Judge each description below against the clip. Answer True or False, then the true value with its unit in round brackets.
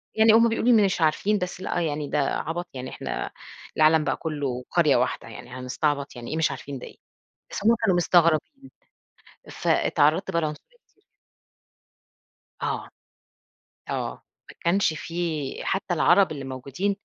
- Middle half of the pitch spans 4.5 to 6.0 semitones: True (5.1 semitones)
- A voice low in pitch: False (160 Hz)